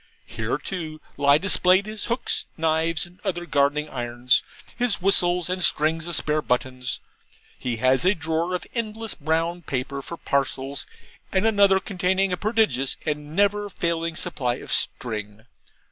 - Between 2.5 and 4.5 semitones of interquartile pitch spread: No, average, 5.1 semitones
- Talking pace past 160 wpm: No, average, 145 wpm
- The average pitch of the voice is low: No, medium, 165 Hz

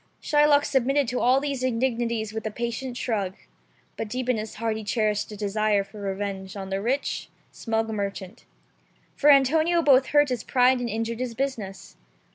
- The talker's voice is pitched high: Yes, high, 230 Hz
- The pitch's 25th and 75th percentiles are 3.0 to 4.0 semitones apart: Yes, average, 3.7 semitones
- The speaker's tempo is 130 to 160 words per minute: No, average, 175 wpm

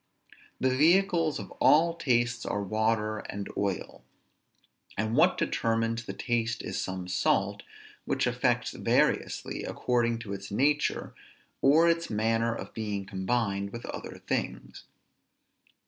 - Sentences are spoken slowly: Yes, slow, 125 wpm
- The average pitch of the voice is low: Yes, low, 115 Hz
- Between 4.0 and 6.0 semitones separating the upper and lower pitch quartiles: Yes, average, 4.5 semitones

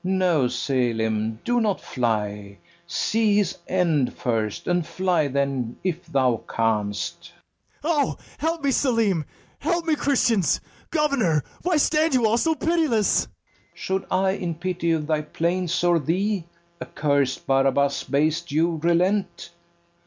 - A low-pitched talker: No, medium, 170 Hz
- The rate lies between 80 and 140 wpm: Yes, slow, 135 wpm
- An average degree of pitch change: No, wide, 7.8 semitones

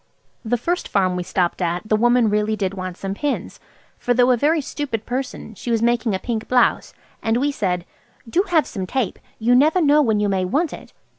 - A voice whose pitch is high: Yes, high, 230 Hz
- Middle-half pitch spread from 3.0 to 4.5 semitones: No, average, 5.1 semitones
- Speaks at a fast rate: Yes, fast, 215 wpm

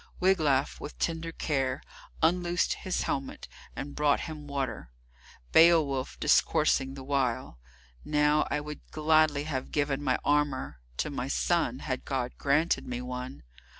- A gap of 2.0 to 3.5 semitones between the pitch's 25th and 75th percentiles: Yes, average, 2.8 semitones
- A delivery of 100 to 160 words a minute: Yes, slow, 135 wpm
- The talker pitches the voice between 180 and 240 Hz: No, medium, 145 Hz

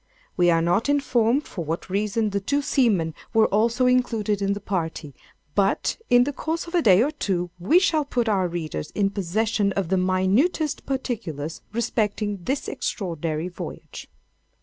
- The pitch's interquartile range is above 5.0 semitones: Yes, wide, 5.6 semitones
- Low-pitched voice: No, high, 205 Hz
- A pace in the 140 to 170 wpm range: Yes, average, 160 wpm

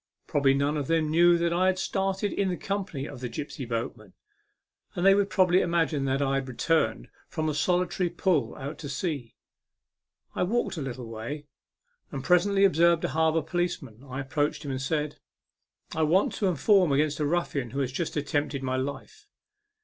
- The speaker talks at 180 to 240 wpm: Yes, average, 190 wpm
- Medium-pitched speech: Yes, medium, 155 Hz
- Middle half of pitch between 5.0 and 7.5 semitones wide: No, average, 4.5 semitones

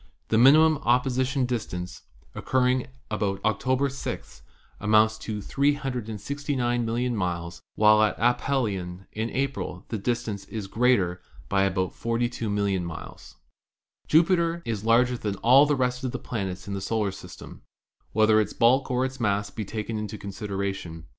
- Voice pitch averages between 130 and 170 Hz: No, low, 110 Hz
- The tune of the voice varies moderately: Yes, average, 4.2 semitones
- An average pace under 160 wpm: Yes, average, 145 wpm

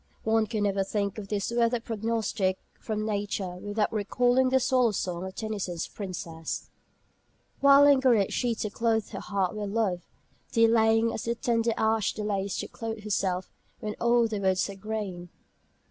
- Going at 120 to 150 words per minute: No, average, 160 wpm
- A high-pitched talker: Yes, high, 215 Hz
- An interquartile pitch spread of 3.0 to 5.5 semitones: No, narrow, 2.6 semitones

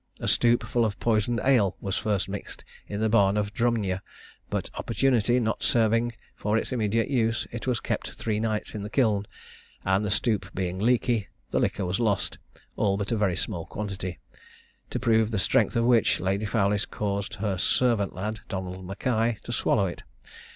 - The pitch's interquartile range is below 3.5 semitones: Yes, average, 2.8 semitones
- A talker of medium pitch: No, low, 105 Hz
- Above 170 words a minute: Yes, average, 180 wpm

